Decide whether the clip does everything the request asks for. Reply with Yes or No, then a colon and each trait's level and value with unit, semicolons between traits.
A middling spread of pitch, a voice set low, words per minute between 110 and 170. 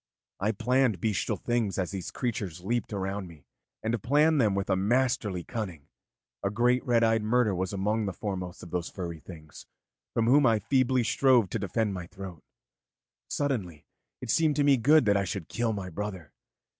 No: average, 4.3 semitones; low, 105 Hz; average, 180 wpm